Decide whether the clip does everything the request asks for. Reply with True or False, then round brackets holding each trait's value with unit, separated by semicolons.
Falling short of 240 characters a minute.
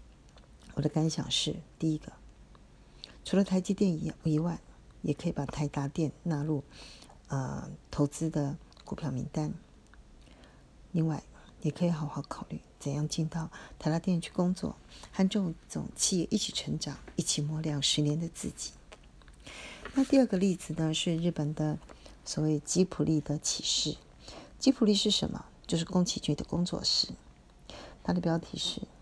True (225 characters per minute)